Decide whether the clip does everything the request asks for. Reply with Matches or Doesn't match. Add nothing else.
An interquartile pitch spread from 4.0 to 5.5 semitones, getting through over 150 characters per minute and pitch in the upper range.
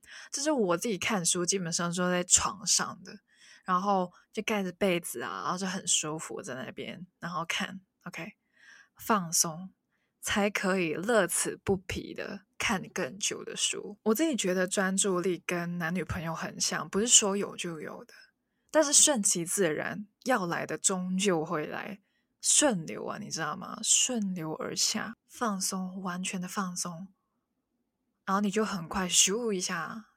Doesn't match